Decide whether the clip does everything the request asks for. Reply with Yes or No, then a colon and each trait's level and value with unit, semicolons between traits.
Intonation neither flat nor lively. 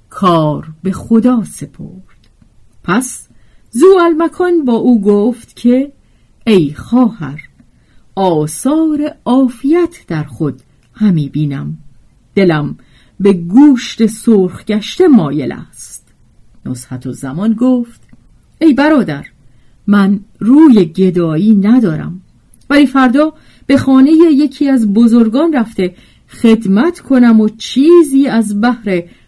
No: wide, 8.2 semitones